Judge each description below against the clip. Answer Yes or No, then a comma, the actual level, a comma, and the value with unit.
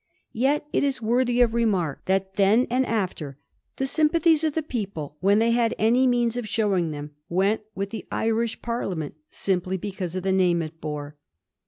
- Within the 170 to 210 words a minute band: Yes, average, 180 wpm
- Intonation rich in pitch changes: No, average, 4.9 semitones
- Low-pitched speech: No, high, 210 Hz